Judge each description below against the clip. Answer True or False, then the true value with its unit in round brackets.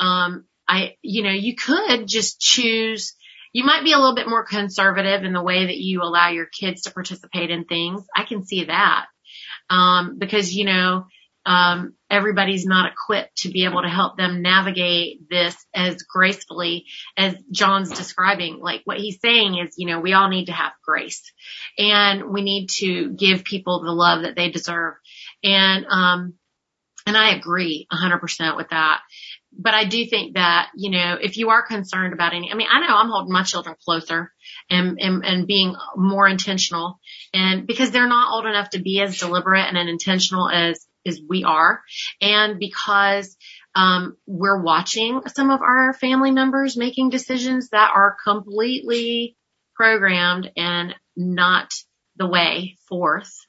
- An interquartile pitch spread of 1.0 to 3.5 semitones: True (2.9 semitones)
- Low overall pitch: False (190 Hz)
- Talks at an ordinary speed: True (170 wpm)